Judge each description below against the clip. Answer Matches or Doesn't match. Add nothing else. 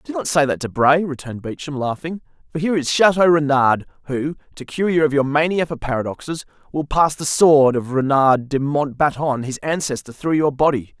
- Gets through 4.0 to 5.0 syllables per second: Doesn't match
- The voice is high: Doesn't match